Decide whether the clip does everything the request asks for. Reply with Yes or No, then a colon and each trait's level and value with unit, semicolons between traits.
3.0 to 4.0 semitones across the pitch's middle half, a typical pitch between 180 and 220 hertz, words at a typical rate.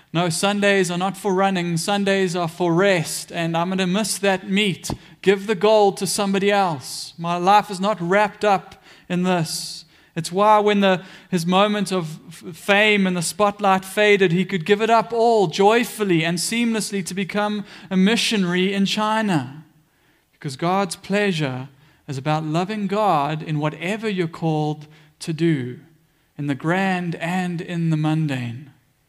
Yes: average, 3.5 semitones; medium, 185 Hz; average, 160 wpm